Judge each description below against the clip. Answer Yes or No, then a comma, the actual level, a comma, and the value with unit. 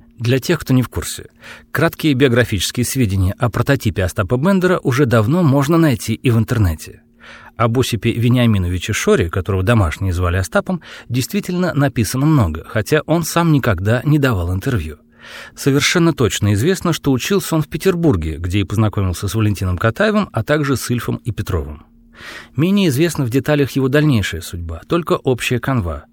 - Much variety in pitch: Yes, wide, 6.3 semitones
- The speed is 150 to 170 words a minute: Yes, average, 155 wpm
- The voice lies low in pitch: Yes, low, 120 Hz